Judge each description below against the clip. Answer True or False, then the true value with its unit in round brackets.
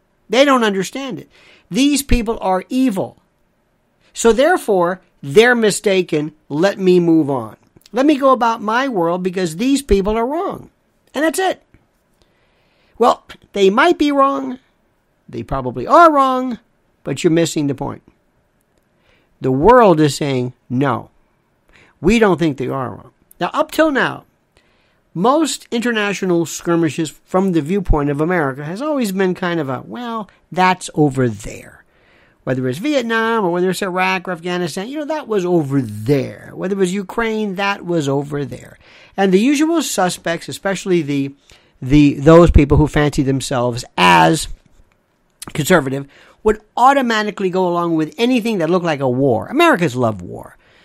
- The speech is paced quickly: False (150 wpm)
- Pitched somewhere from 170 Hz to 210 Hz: True (185 Hz)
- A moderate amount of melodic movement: False (7.5 semitones)